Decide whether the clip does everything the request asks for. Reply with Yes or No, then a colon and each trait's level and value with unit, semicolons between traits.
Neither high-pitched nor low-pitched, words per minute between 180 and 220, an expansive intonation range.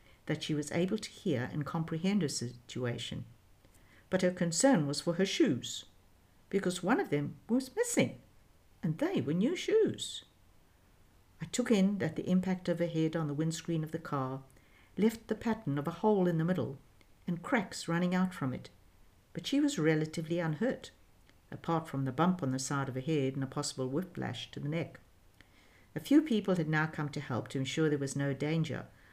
Yes: medium, 150 Hz; average, 195 wpm; wide, 6.8 semitones